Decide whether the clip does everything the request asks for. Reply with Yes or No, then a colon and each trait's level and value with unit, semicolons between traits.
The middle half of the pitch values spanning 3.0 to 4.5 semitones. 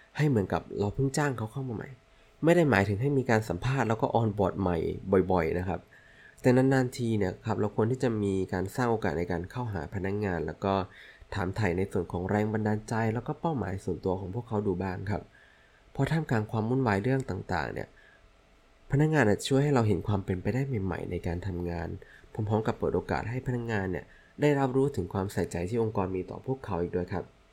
No: average, 5.3 semitones